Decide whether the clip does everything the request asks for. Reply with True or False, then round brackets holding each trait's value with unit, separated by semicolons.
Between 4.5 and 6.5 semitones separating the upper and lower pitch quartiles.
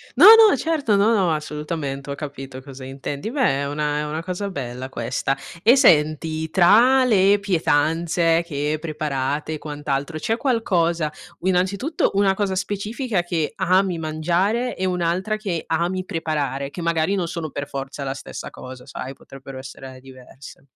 True (5.2 semitones)